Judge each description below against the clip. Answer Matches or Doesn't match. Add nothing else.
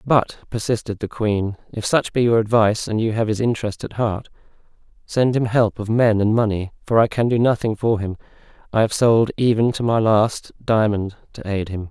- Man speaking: Matches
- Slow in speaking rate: Doesn't match